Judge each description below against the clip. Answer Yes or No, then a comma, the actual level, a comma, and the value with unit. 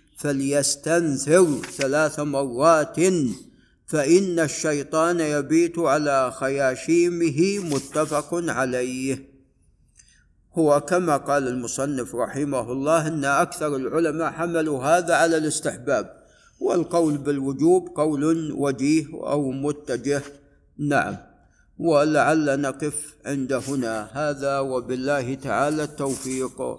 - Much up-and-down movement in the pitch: No, average, 2.7 semitones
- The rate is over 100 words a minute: No, average, 85 wpm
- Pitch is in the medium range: Yes, medium, 145 Hz